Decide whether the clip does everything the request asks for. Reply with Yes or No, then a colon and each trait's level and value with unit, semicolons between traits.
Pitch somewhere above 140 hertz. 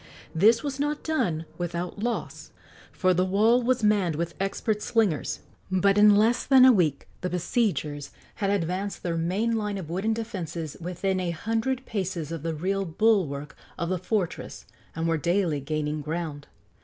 Yes: medium, 185 Hz